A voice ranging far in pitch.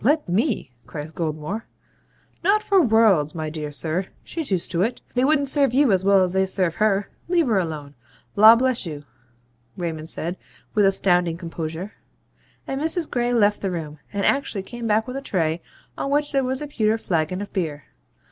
Yes: wide, 7.2 semitones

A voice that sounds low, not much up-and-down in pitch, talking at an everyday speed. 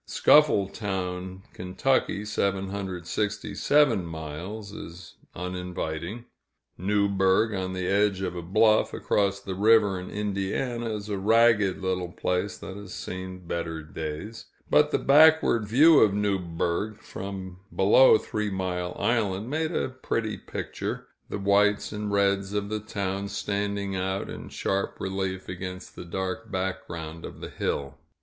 No: low, 100 Hz; narrow, 2.3 semitones; slow, 130 wpm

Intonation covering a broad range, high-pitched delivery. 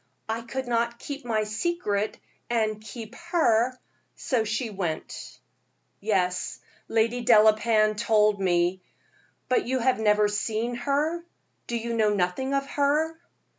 No: average, 3.1 semitones; high, 225 Hz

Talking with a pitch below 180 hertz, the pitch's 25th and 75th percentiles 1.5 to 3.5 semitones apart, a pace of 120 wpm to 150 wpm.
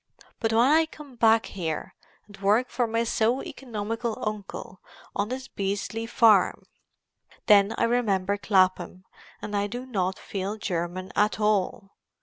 No: high, 210 Hz; average, 3.0 semitones; average, 140 wpm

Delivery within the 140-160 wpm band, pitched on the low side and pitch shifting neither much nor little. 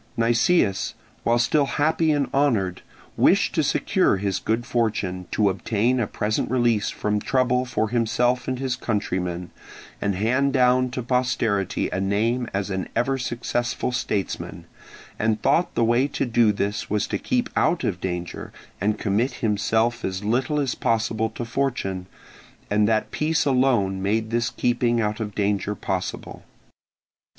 Yes: average, 150 wpm; low, 115 Hz; average, 3.6 semitones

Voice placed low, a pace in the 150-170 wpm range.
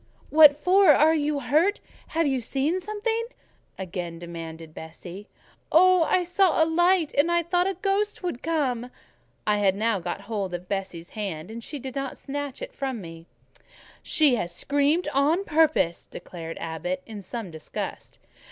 No: very high, 270 Hz; average, 165 wpm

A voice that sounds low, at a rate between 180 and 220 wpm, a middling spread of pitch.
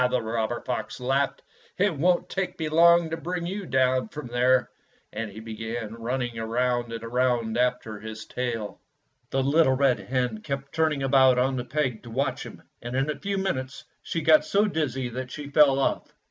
Yes: low, 130 Hz; average, 190 wpm; average, 3.9 semitones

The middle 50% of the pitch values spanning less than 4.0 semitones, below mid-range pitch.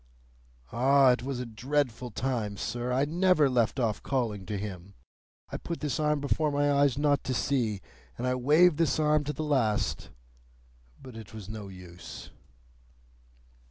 No: average, 4.7 semitones; low, 130 Hz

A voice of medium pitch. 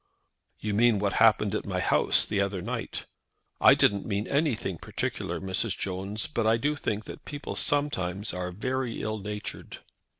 No: low, 105 Hz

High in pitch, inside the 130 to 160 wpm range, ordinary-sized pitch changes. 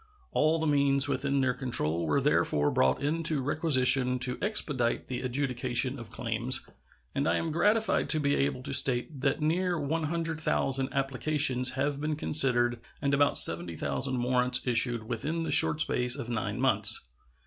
No: low, 135 Hz; average, 155 wpm; average, 3.5 semitones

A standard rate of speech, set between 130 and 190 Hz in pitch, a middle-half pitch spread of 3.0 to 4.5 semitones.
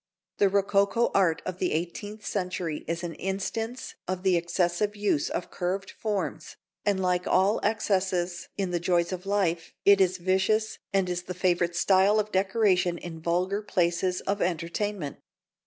No: average, 155 wpm; medium, 185 Hz; narrow, 2.4 semitones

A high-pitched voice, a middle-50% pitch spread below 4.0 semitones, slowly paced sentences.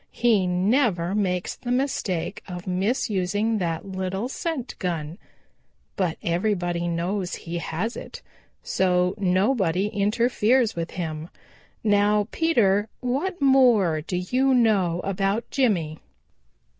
No: high, 195 Hz; average, 4.5 semitones; slow, 110 wpm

